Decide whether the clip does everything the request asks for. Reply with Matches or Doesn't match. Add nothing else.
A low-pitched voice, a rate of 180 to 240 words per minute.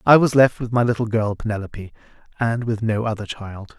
Matches